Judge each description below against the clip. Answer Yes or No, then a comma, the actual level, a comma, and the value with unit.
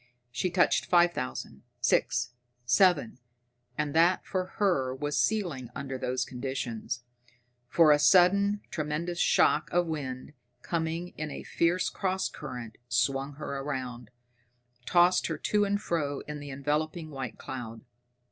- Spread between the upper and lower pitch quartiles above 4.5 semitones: Yes, average, 5.1 semitones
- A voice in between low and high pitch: Yes, medium, 150 Hz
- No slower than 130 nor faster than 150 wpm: Yes, slow, 135 wpm